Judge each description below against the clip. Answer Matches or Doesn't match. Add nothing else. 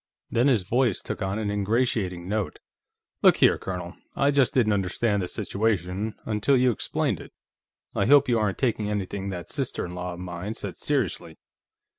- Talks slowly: Doesn't match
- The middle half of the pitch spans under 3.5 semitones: Doesn't match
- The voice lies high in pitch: Doesn't match